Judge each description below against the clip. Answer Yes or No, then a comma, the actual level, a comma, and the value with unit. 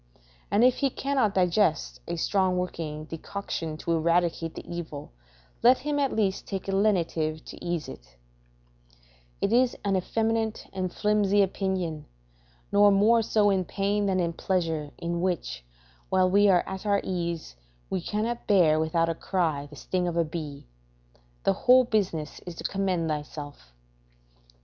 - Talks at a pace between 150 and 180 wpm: Yes, average, 155 wpm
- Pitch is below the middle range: No, medium, 185 Hz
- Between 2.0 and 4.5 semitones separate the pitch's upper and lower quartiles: Yes, average, 3.8 semitones